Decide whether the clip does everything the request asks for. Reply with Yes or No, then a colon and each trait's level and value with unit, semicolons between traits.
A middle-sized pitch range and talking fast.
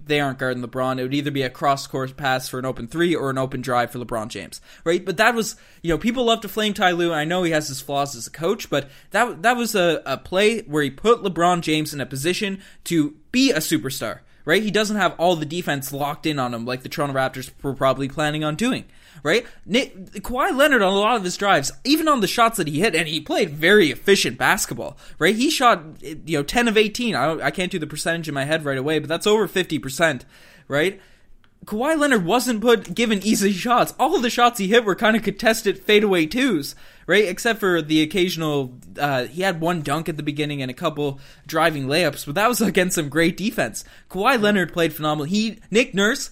No: wide, 6.7 semitones; fast, 235 wpm